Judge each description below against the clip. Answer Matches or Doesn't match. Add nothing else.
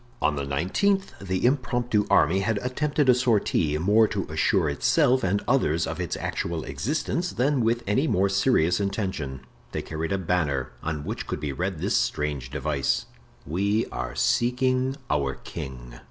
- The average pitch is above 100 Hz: Doesn't match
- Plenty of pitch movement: Matches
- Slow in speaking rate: Doesn't match